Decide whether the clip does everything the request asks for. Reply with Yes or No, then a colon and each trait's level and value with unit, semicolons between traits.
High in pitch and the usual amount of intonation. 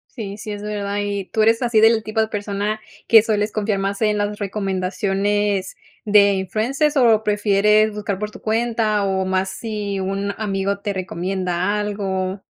No: high, 205 Hz; narrow, 1.6 semitones